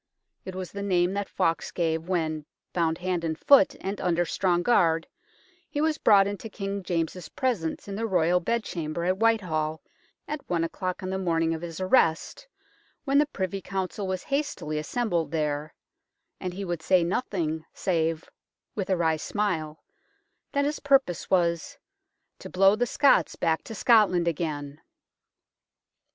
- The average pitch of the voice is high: No, medium, 180 Hz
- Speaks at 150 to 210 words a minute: Yes, average, 160 wpm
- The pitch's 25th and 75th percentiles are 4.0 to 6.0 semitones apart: No, average, 3.6 semitones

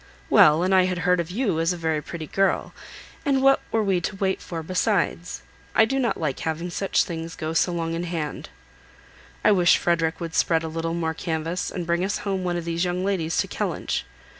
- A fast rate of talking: Yes, fast, 215 wpm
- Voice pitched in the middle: Yes, medium, 175 Hz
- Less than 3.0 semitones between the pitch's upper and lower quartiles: Yes, narrow, 2.4 semitones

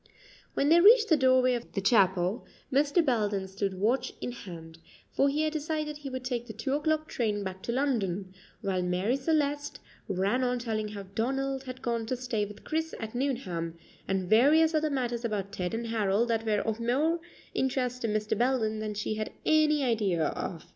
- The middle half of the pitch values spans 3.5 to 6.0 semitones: Yes, average, 5.0 semitones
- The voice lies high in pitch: Yes, high, 235 Hz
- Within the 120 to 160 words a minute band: No, average, 190 wpm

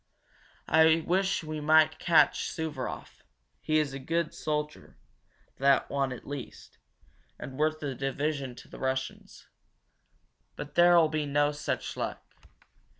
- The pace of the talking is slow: Yes, slow, 130 wpm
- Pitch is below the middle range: No, medium, 150 Hz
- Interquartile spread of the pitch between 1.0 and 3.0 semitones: Yes, narrow, 2.4 semitones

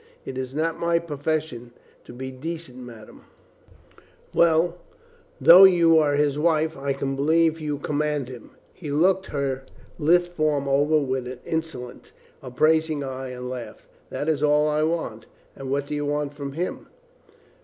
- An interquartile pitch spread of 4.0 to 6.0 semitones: No, average, 3.2 semitones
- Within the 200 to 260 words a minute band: No, average, 165 wpm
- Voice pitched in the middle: Yes, medium, 150 Hz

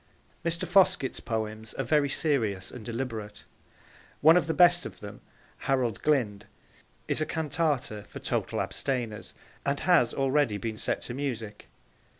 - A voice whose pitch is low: Yes, low, 130 Hz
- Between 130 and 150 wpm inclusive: Yes, average, 145 wpm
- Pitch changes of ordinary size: No, wide, 5.8 semitones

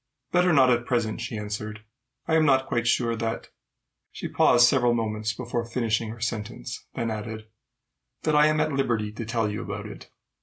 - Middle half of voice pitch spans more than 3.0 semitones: No, narrow, 2.6 semitones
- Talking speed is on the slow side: No, average, 190 wpm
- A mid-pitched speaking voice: No, low, 120 Hz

